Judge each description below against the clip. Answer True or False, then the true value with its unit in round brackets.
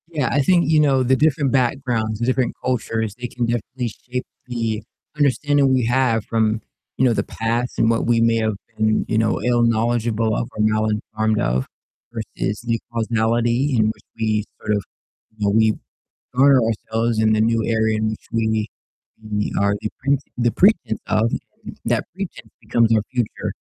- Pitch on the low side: True (115 Hz)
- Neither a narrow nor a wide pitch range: False (2.3 semitones)